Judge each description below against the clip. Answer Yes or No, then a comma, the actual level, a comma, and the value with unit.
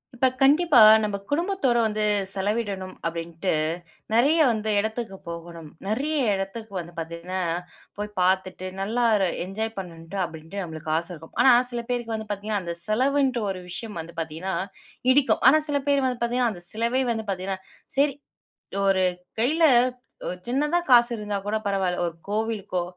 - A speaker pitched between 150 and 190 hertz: No, high, 210 Hz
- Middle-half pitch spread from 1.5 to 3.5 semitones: No, average, 5.0 semitones